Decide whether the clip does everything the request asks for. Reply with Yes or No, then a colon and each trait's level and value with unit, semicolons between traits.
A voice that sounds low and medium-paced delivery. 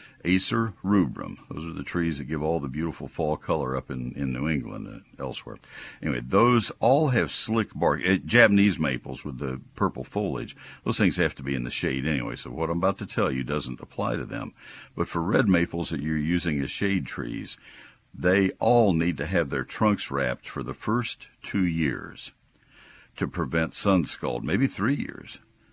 Yes: very low, 80 Hz; average, 195 wpm